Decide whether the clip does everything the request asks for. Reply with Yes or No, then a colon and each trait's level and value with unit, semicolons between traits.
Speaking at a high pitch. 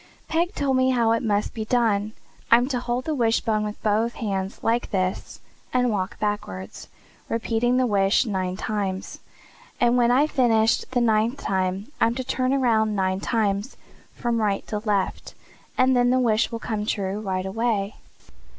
Yes: high, 225 Hz